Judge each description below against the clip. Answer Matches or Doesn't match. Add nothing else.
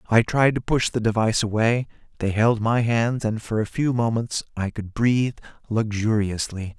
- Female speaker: Doesn't match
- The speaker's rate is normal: Matches